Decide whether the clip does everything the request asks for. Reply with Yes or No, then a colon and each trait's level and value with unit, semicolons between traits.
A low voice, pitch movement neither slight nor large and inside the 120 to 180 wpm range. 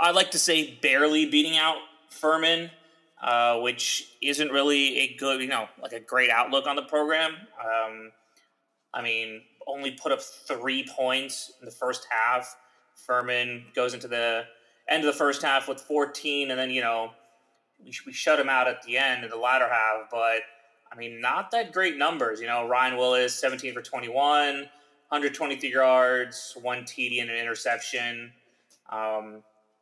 Yes: low, 130 Hz; average, 3.7 semitones; average, 170 wpm